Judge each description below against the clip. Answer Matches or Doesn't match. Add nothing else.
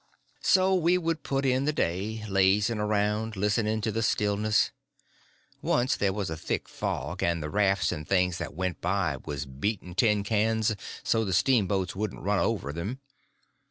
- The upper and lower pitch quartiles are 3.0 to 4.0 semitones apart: Matches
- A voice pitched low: Matches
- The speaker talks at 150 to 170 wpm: Matches